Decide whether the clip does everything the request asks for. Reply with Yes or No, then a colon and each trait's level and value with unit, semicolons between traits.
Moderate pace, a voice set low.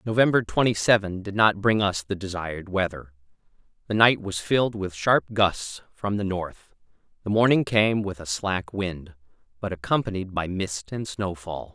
Yes: average, 170 wpm; low, 100 Hz